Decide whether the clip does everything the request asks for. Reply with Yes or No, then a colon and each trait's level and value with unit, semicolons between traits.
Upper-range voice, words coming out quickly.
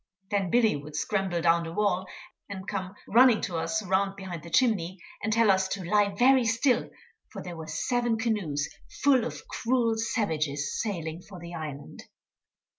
No: high, 195 Hz; average, 170 wpm